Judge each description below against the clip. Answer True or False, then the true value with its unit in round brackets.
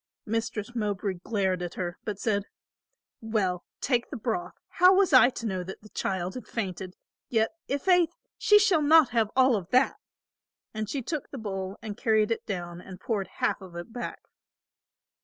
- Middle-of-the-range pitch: False (220 Hz)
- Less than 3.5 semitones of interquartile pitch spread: False (5.1 semitones)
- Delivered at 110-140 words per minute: False (175 wpm)